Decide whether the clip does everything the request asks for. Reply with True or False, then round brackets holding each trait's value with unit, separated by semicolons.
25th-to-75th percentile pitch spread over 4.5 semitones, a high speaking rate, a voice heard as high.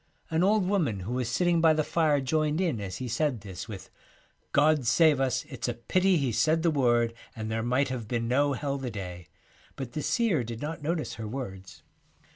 False (5.2 semitones; 215 wpm; 130 Hz)